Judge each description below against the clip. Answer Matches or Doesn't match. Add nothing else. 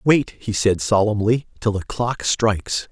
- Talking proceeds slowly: Doesn't match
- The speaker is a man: Matches